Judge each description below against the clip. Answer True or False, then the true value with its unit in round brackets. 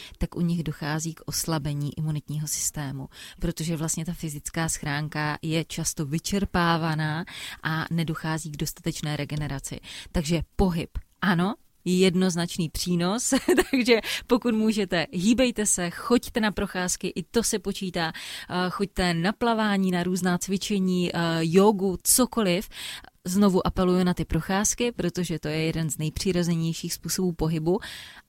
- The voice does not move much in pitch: False (3.4 semitones)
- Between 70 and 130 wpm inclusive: True (125 wpm)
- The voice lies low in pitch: False (175 Hz)